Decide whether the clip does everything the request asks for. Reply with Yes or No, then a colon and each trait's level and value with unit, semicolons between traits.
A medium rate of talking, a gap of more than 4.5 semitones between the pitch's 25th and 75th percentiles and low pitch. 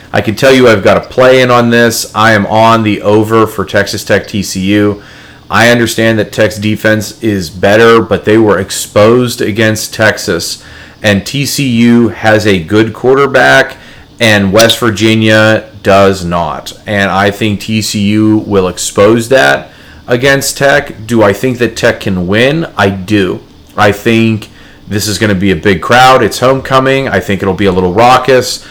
No: average, 170 wpm; average, 2.9 semitones; low, 110 Hz